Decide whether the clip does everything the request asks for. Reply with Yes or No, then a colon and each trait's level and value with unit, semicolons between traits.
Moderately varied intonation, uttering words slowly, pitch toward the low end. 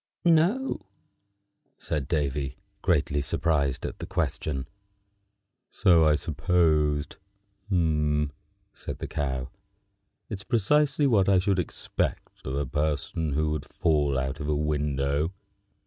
Yes: average, 3.7 semitones; slow, 115 wpm; very low, 75 Hz